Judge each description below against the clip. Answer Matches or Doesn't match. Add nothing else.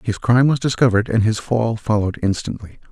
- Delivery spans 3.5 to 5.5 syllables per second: Doesn't match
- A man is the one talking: Matches